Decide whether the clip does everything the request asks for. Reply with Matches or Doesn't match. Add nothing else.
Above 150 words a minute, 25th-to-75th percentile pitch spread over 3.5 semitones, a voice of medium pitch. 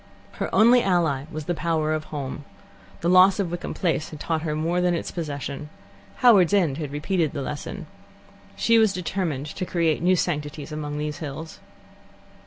Doesn't match